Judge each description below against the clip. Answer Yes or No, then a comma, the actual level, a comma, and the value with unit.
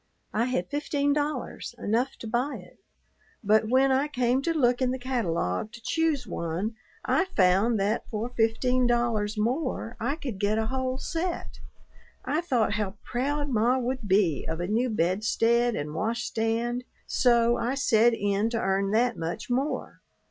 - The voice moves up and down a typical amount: Yes, average, 3.4 semitones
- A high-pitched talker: Yes, high, 235 Hz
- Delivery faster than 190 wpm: No, average, 165 wpm